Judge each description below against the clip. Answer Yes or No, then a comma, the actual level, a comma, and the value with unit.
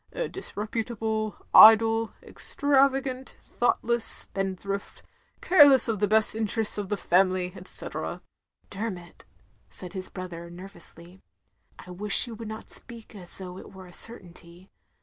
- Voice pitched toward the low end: No, high, 210 Hz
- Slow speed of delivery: Yes, slow, 130 wpm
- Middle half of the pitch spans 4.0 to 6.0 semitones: No, average, 3.6 semitones